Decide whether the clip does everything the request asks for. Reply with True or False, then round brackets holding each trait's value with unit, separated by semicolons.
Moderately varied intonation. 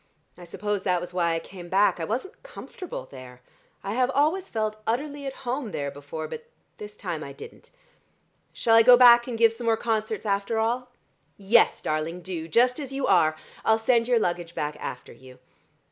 False (6.1 semitones)